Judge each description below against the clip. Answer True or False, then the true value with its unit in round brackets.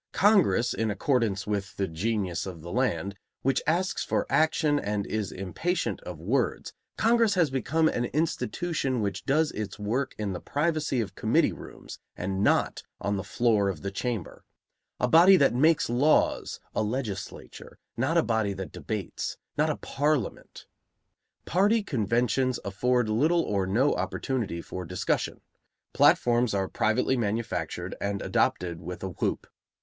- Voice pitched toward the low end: True (115 Hz)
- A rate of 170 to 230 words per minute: False (150 wpm)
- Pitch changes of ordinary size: False (6.6 semitones)